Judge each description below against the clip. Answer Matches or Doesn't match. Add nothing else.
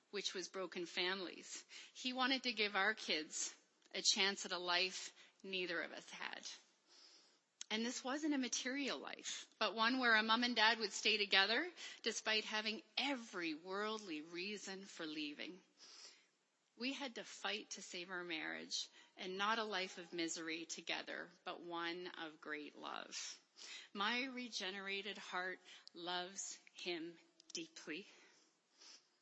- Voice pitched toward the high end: Matches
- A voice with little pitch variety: Doesn't match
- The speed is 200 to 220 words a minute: Doesn't match